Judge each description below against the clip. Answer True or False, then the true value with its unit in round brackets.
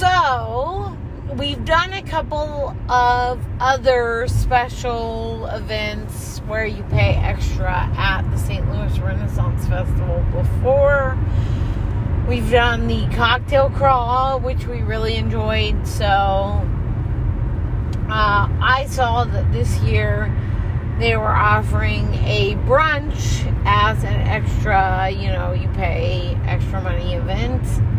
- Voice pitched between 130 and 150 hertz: False (105 Hz)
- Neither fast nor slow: False (110 wpm)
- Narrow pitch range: True (1.8 semitones)